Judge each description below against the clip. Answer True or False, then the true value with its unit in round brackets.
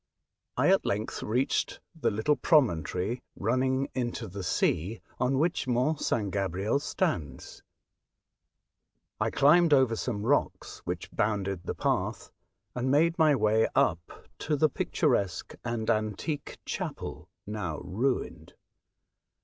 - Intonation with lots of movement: True (5.8 semitones)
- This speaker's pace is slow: True (120 wpm)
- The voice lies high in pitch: False (115 Hz)